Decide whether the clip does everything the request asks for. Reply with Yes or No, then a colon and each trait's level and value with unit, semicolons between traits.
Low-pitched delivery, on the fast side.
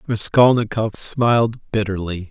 No: low, 110 Hz; slow, 80 wpm